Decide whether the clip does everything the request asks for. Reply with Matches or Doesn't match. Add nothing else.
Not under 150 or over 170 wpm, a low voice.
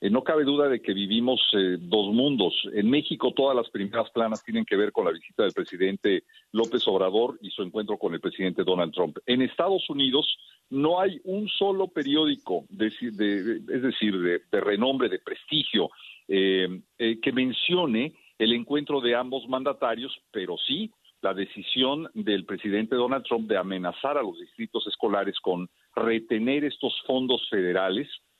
Matches